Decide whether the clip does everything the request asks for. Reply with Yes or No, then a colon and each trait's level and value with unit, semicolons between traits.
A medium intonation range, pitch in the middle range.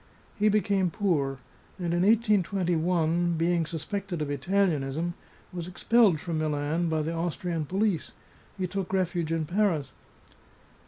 Yes: average, 3.4 semitones; medium, 175 Hz